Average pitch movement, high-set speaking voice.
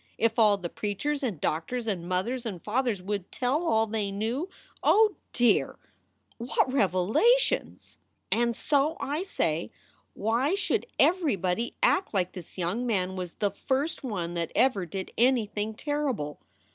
No: wide, 6.1 semitones; high, 225 Hz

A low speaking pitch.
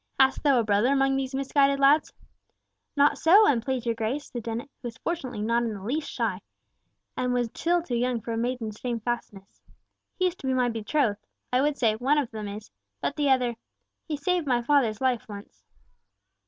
No: very high, 250 Hz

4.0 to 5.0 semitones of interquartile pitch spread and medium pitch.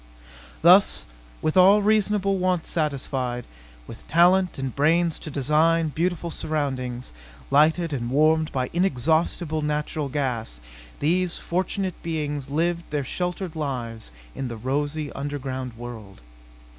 Yes: average, 4.4 semitones; medium, 150 Hz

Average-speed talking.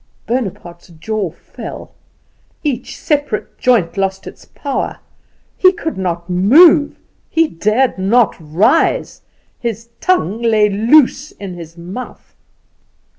No: slow, 110 wpm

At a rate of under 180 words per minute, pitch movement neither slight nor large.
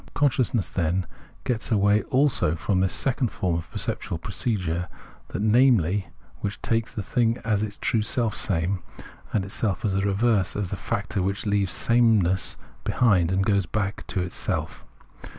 Yes: average, 150 wpm; average, 3.2 semitones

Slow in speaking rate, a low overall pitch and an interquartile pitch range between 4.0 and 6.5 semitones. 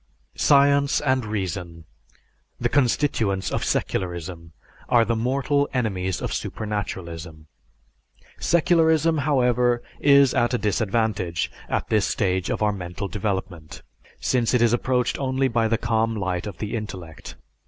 Yes: slow, 130 wpm; low, 110 Hz; wide, 5.5 semitones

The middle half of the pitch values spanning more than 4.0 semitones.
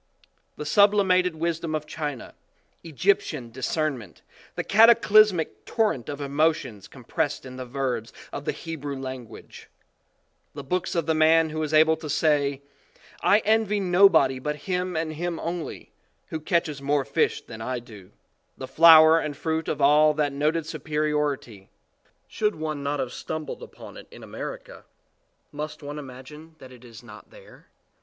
No: average, 3.2 semitones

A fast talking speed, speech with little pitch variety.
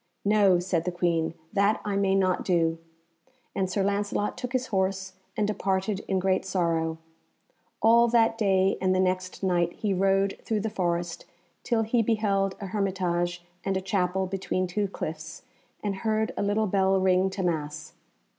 No: average, 165 wpm; narrow, 2.2 semitones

